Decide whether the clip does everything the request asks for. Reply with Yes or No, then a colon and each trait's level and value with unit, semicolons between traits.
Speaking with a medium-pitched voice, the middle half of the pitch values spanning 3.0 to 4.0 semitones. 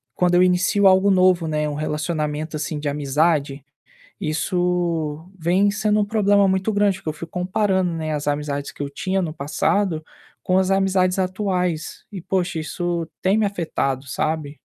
Yes: medium, 175 Hz; average, 3.7 semitones